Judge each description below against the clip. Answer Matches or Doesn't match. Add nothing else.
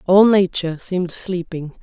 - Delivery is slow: Matches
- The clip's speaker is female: Matches